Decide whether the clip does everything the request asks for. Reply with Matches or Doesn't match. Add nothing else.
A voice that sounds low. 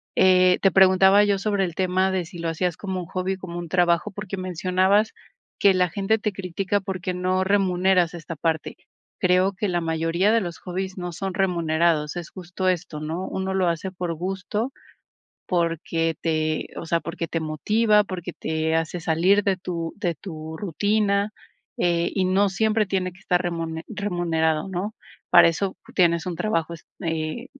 Doesn't match